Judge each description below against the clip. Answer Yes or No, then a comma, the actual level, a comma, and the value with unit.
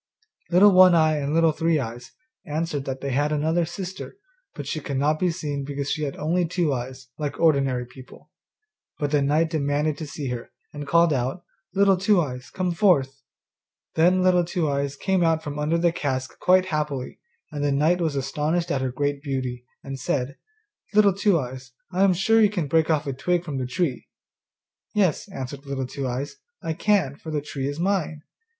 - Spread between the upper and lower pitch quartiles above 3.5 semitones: Yes, average, 3.9 semitones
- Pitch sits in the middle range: Yes, medium, 150 Hz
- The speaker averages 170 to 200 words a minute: Yes, average, 195 wpm